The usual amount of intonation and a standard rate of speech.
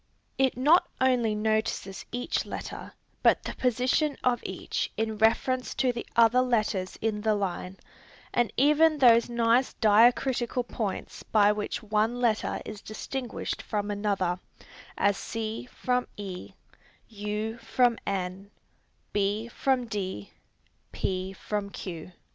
No: average, 3.3 semitones; slow, 125 wpm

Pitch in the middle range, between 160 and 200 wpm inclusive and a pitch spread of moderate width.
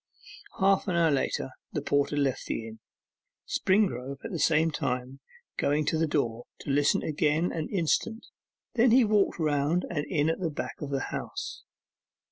Yes: medium, 150 Hz; average, 170 wpm; average, 4.0 semitones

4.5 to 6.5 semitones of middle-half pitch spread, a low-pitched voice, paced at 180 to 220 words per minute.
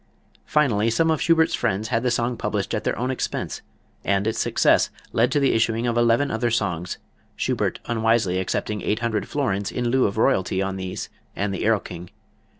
No: average, 3.3 semitones; low, 115 Hz; average, 185 wpm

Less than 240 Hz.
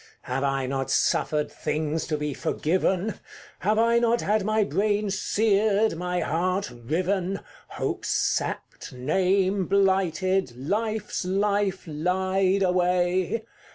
Yes: medium, 185 Hz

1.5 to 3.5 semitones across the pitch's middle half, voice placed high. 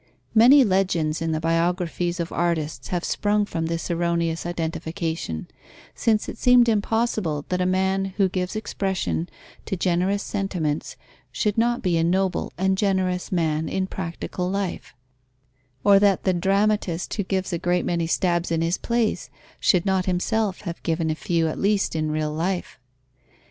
No: average, 2.9 semitones; medium, 180 Hz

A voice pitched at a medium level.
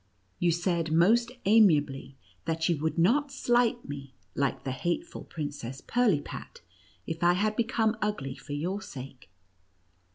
Yes: medium, 170 Hz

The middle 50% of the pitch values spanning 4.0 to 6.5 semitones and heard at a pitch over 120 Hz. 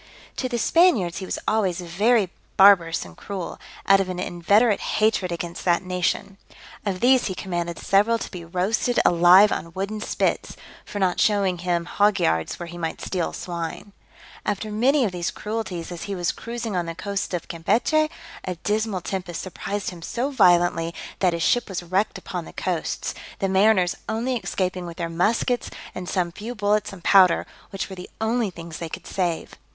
No: average, 3.5 semitones; high, 190 Hz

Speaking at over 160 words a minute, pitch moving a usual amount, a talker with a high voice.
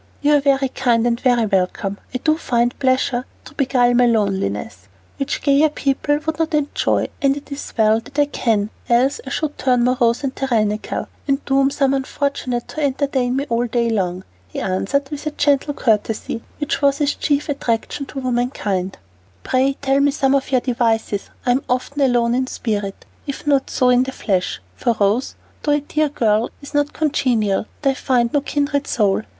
Yes: average, 185 wpm; average, 3.4 semitones; very high, 255 Hz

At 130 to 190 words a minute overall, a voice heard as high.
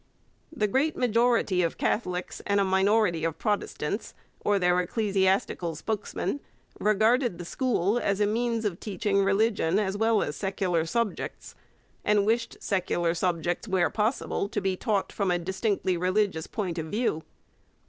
Yes: average, 150 wpm; high, 200 Hz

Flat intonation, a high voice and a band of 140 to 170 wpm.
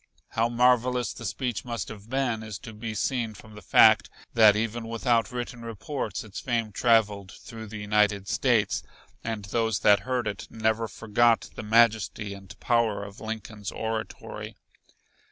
No: narrow, 2.0 semitones; low, 110 Hz; average, 155 wpm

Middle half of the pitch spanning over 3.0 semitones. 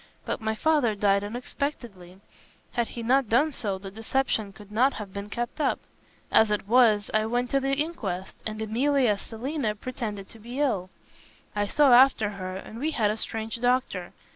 Yes: average, 3.8 semitones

